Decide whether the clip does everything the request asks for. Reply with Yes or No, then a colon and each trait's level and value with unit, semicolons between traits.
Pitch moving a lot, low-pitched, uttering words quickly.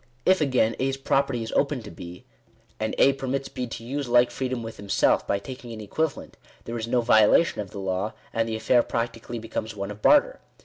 No: average, 3.5 semitones; low, 115 Hz; fast, 210 wpm